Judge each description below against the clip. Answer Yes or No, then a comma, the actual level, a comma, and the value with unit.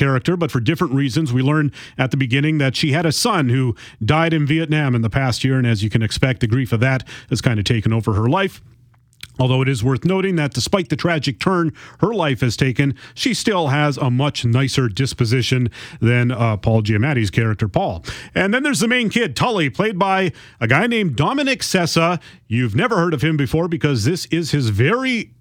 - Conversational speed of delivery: No, fast, 215 wpm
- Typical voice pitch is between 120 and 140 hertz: Yes, low, 135 Hz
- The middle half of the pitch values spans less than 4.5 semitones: No, average, 4.9 semitones